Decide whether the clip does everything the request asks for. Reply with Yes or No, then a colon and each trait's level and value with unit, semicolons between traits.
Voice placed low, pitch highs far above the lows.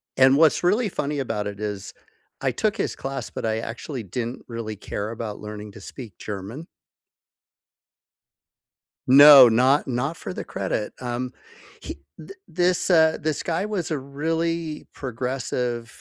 Yes: low, 130 Hz; wide, 5.8 semitones